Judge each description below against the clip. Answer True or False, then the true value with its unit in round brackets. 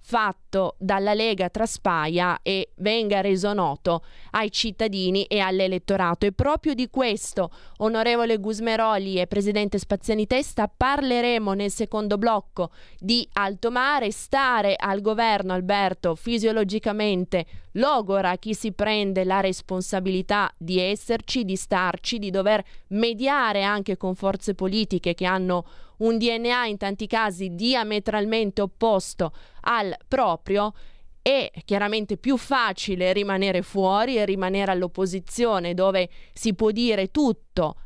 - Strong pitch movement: False (2.9 semitones)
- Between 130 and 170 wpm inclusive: False (120 wpm)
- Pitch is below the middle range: False (205 Hz)